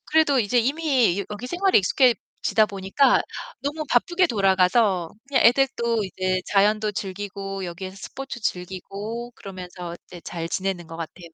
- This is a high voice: Yes, high, 205 Hz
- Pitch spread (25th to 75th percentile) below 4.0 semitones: No, average, 4.9 semitones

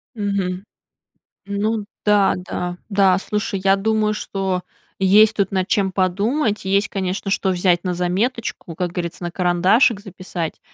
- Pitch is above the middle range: Yes, high, 195 Hz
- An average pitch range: No, narrow, 2.3 semitones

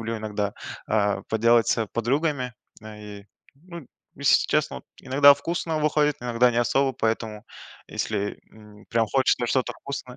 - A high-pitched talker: No, low, 120 Hz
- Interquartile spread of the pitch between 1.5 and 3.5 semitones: No, average, 4.2 semitones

